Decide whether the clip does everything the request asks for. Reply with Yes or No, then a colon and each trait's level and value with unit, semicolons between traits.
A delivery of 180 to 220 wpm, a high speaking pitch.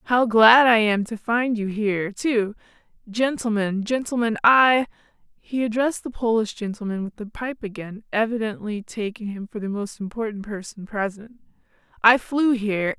No: average, 150 wpm; high, 220 Hz